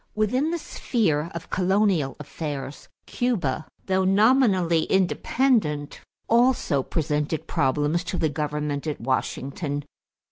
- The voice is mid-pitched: Yes, medium, 165 Hz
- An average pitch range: No, wide, 6.1 semitones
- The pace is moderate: No, slow, 110 wpm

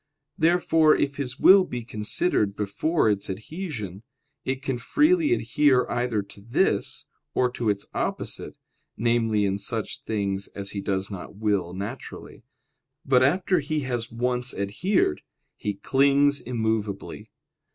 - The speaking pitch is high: No, low, 120 Hz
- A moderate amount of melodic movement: No, wide, 5.8 semitones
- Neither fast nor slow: No, slow, 130 wpm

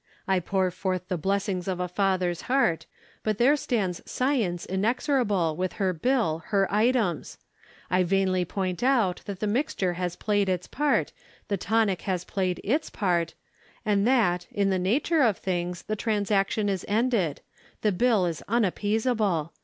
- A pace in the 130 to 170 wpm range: Yes, average, 155 wpm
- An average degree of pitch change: Yes, average, 3.5 semitones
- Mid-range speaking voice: No, high, 195 Hz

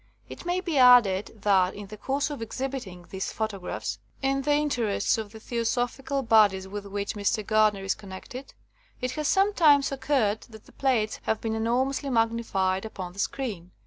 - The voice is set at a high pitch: Yes, high, 225 Hz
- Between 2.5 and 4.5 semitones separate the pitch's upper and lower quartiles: No, average, 5.0 semitones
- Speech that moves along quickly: No, average, 175 wpm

